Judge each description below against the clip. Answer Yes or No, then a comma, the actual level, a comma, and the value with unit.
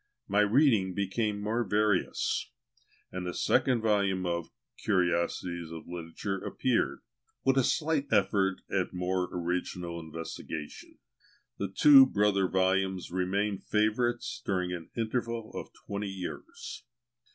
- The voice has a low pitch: Yes, very low, 95 Hz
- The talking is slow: Yes, slow, 120 wpm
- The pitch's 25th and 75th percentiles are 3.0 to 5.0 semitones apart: Yes, average, 3.3 semitones